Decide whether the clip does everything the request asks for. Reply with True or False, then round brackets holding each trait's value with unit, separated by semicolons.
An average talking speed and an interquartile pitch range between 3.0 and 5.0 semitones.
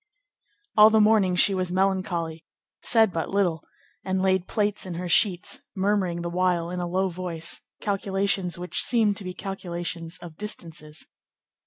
False (155 wpm; 2.4 semitones)